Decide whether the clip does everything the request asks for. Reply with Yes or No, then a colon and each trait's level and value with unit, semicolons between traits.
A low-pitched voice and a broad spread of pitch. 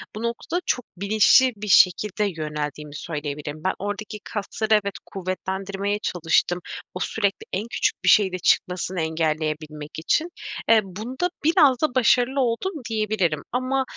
No: high, 200 Hz; wide, 5.8 semitones